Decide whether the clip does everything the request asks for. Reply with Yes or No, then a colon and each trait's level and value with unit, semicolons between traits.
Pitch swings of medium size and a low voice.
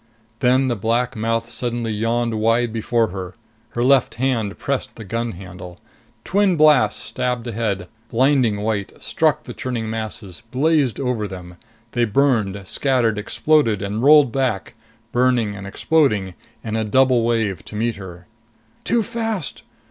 Yes: average, 3.7 semitones; low, 115 Hz